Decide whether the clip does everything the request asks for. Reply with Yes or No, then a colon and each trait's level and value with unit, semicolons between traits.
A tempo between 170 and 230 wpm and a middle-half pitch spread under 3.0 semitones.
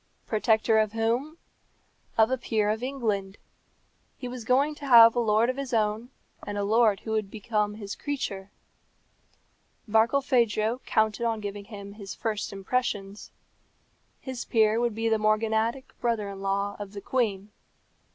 No: average, 150 wpm; narrow, 2.5 semitones